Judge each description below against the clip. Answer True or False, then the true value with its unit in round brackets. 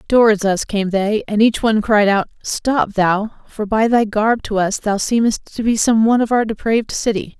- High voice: True (215 Hz)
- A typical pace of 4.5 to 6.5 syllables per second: True (4.9 syllables/s)